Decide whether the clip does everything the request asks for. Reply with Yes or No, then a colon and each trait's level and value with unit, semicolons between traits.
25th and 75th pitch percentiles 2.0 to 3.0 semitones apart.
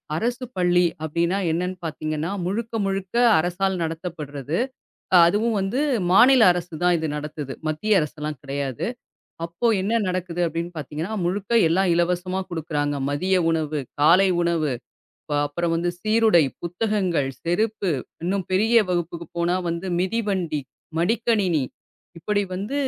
No: average, 3.6 semitones